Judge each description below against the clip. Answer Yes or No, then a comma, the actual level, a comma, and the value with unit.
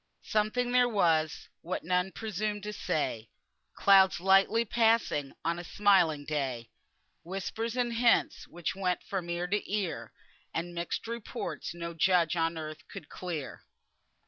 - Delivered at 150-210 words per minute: No, average, 140 wpm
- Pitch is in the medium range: Yes, medium, 180 Hz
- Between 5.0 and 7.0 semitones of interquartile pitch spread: No, average, 4.2 semitones